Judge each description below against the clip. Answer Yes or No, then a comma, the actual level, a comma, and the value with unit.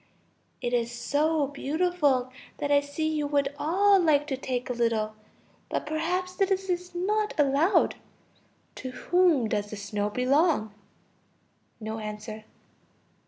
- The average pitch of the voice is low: No, very high, 285 Hz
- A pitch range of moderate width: No, wide, 6.6 semitones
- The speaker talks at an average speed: No, slow, 130 wpm